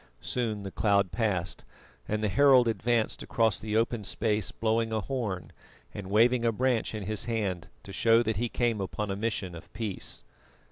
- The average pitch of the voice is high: No, low, 110 Hz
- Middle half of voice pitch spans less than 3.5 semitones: Yes, narrow, 2.5 semitones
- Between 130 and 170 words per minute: No, average, 180 wpm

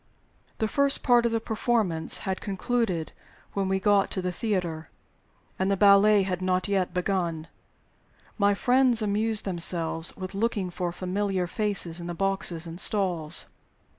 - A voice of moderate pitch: No, high, 195 Hz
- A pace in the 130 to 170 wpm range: Yes, average, 150 wpm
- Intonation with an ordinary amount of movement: Yes, average, 3.1 semitones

